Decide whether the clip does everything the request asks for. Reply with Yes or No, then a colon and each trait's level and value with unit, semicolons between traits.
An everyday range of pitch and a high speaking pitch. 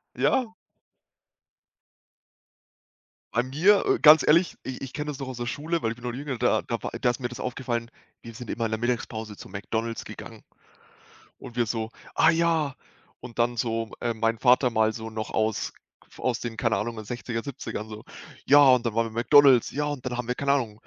No: average, 3.2 semitones; low, 120 Hz